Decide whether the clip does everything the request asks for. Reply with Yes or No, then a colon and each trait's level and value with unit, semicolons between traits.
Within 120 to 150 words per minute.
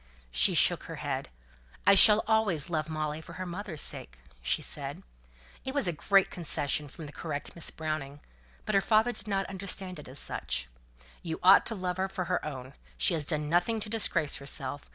No: average, 200 wpm